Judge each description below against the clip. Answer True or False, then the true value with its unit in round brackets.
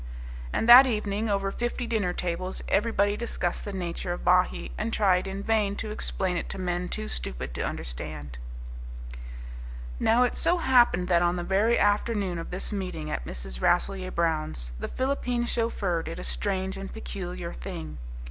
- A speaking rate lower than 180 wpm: True (165 wpm)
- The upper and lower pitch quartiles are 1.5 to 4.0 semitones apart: False (4.5 semitones)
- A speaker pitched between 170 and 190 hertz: True (185 Hz)